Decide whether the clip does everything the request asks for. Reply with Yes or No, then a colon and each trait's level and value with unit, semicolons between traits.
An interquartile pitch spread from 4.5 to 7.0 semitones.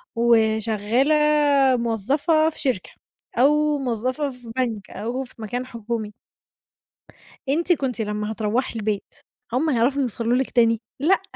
No: average, 3.6 semitones